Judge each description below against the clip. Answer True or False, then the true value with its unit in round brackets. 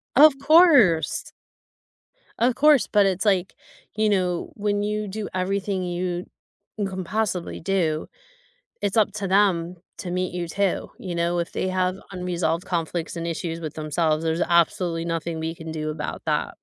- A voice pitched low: False (180 Hz)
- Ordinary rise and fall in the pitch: True (3.3 semitones)